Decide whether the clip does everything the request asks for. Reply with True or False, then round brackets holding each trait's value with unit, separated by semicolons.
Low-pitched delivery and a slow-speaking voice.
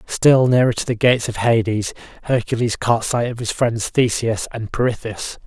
False (115 Hz; 175 wpm)